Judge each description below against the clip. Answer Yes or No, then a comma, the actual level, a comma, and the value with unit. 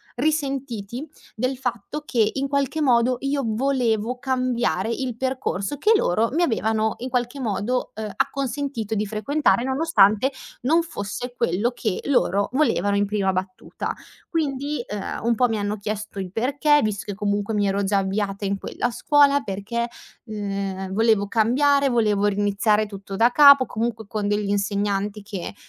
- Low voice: No, high, 225 Hz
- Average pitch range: Yes, average, 4.6 semitones